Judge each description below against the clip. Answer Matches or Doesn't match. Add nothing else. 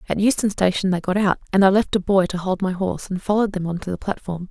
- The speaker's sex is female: Matches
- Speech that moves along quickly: Matches